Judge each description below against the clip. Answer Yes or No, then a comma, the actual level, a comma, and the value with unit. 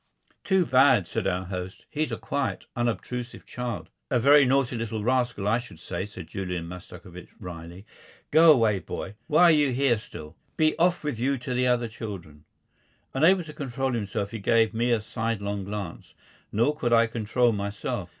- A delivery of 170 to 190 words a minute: Yes, average, 175 wpm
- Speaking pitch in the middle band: No, low, 115 Hz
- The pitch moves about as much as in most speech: Yes, average, 4.7 semitones